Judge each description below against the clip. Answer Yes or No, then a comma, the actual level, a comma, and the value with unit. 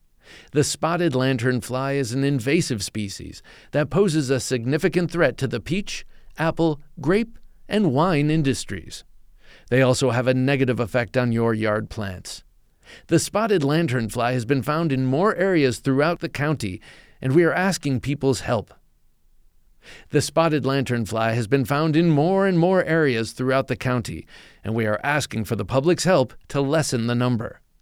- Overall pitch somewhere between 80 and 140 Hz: Yes, low, 135 Hz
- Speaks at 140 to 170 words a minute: Yes, average, 165 wpm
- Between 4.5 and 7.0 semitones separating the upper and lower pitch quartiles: Yes, average, 4.8 semitones